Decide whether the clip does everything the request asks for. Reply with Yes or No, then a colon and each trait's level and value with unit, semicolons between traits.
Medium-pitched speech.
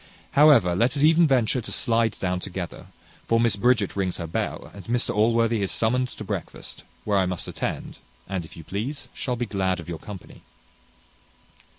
No: low, 110 Hz